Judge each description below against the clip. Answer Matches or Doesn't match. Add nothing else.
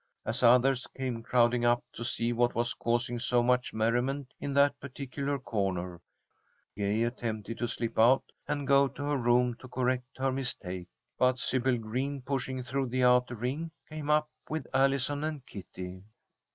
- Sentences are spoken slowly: Doesn't match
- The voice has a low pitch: Matches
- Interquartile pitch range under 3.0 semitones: Matches